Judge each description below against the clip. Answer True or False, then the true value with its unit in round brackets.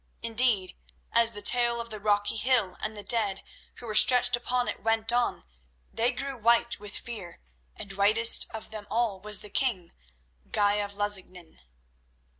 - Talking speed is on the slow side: False (165 wpm)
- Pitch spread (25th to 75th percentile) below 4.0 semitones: True (2.6 semitones)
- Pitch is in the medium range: False (220 Hz)